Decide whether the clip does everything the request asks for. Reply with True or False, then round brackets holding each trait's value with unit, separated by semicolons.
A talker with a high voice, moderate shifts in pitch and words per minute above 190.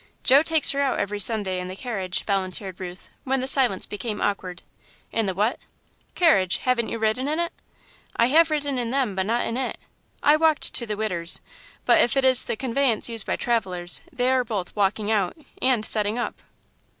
True (230 Hz; 5.0 semitones; 200 wpm)